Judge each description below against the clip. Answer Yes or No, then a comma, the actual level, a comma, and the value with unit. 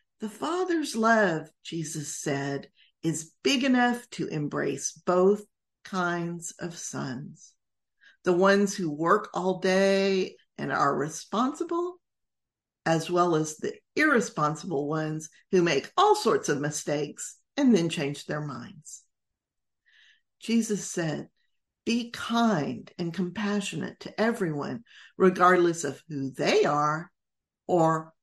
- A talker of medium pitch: Yes, medium, 180 Hz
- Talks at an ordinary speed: No, slow, 115 wpm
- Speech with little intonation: No, average, 5.2 semitones